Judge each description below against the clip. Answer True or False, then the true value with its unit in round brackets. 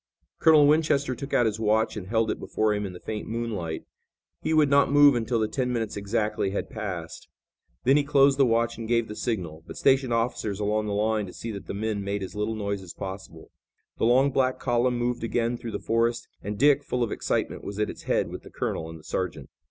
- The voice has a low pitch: True (110 Hz)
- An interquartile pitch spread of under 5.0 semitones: True (3.5 semitones)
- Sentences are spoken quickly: True (230 wpm)